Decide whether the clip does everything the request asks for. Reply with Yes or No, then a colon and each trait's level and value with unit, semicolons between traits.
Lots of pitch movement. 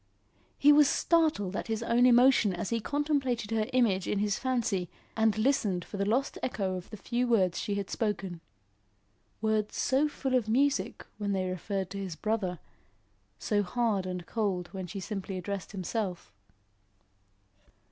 No: average, 4.1 semitones